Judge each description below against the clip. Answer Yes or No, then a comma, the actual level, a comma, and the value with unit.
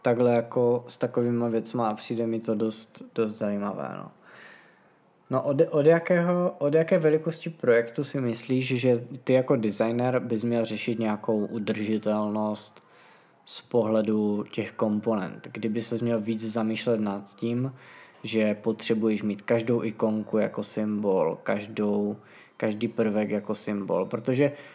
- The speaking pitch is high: No, low, 115 Hz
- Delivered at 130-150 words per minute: Yes, average, 135 wpm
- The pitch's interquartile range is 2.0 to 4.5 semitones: Yes, narrow, 2.5 semitones